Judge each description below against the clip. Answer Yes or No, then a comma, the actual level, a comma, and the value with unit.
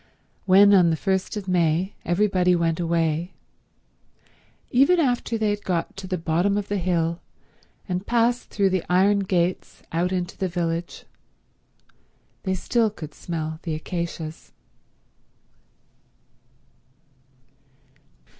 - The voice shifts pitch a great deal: No, average, 3.0 semitones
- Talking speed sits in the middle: No, slow, 115 wpm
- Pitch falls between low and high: Yes, medium, 180 Hz